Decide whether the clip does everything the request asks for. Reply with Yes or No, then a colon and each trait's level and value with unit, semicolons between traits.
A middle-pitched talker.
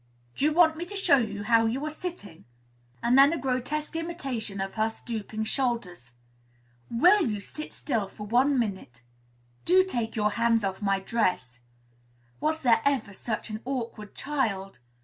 No: high, 230 Hz